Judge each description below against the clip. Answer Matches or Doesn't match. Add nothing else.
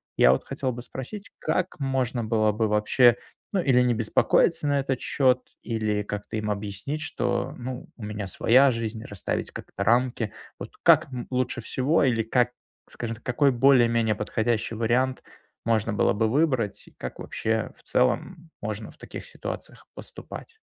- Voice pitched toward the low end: Matches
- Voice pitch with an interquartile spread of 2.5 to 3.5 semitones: Matches